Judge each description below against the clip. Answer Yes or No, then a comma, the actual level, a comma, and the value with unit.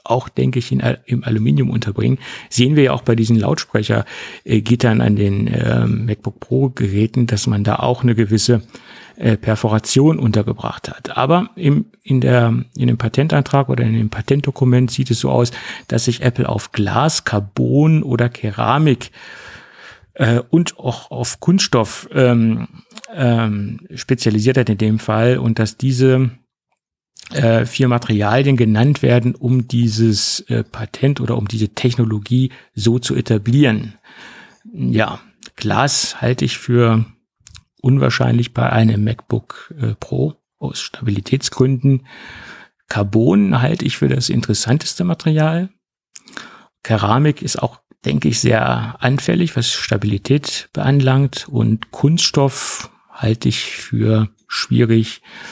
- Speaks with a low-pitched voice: Yes, low, 120 Hz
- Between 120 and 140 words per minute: Yes, average, 130 wpm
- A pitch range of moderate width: Yes, average, 3.2 semitones